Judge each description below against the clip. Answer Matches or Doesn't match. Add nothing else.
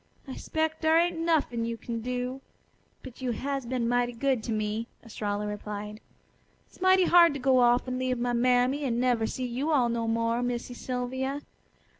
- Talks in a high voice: Matches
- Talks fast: Doesn't match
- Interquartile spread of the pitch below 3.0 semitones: Matches